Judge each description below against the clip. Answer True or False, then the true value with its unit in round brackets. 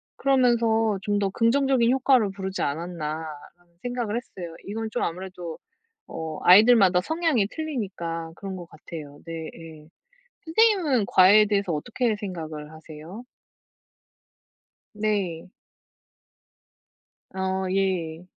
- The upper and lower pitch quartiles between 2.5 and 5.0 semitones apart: False (5.6 semitones)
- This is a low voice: False (190 Hz)